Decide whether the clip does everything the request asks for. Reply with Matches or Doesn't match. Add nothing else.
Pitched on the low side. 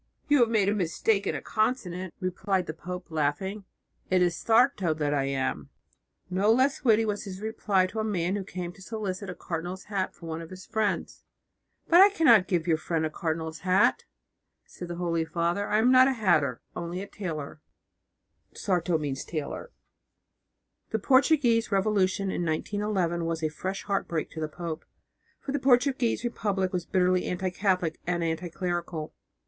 Doesn't match